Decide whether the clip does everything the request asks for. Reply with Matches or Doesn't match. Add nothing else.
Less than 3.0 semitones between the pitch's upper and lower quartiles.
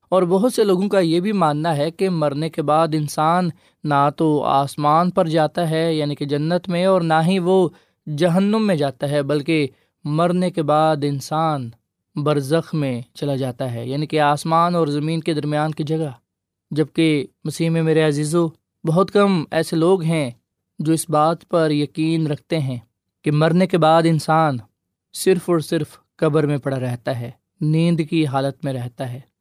Matches